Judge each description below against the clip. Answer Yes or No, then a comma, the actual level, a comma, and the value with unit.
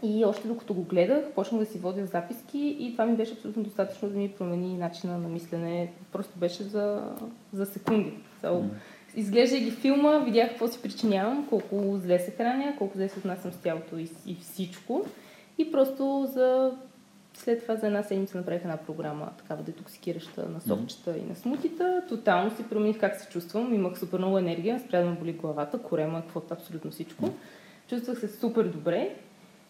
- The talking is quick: Yes, fast, 175 wpm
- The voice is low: No, high, 200 Hz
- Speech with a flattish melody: No, average, 4.7 semitones